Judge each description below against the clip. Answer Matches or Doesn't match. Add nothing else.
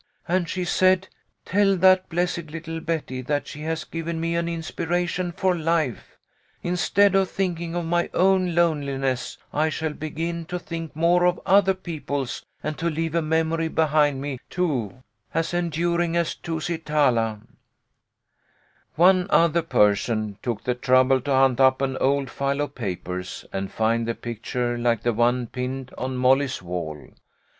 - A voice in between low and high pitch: Matches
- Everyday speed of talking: Matches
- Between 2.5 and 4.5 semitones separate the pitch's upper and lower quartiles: Doesn't match